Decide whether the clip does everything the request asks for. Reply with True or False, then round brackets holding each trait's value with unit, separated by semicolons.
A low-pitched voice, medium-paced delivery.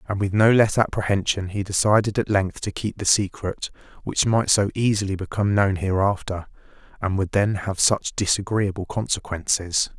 True (100 Hz; 160 wpm)